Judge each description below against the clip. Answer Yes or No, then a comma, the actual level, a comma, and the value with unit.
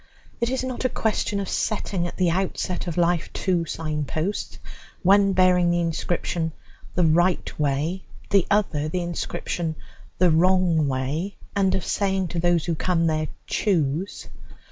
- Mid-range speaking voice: Yes, medium, 175 Hz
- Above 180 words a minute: No, average, 155 wpm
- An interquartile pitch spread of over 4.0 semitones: No, average, 2.8 semitones